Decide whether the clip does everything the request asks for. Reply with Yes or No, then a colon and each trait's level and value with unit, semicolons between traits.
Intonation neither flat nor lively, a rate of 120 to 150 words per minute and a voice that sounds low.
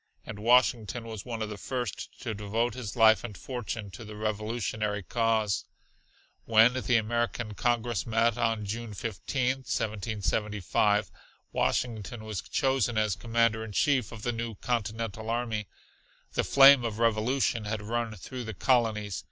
No: narrow, 2.0 semitones; average, 145 wpm; low, 115 Hz